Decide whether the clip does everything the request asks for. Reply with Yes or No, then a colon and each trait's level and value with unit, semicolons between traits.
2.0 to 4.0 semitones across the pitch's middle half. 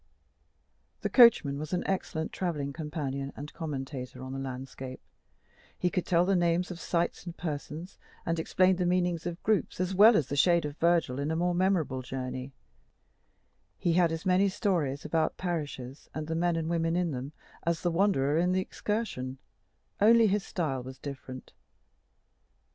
No: average, 4.4 semitones